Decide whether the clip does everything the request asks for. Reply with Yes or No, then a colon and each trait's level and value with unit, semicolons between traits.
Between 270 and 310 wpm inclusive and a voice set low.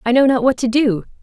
No: fast, 295 wpm; high, 245 Hz